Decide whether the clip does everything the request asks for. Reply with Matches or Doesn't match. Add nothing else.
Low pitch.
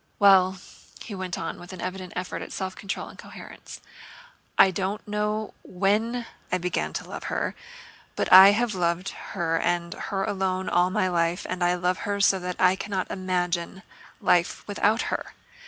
Doesn't match